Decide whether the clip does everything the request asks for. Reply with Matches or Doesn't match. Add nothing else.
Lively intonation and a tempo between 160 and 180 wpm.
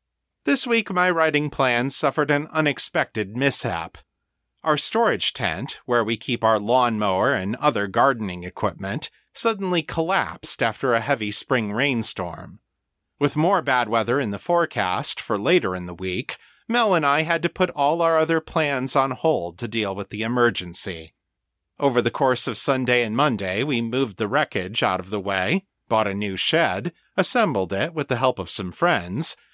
Matches